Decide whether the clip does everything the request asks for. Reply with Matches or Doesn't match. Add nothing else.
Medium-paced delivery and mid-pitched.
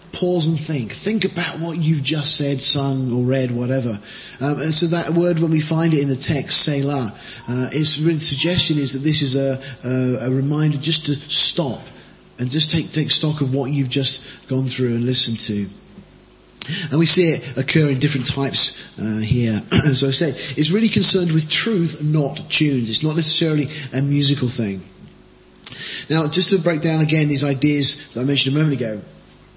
Matches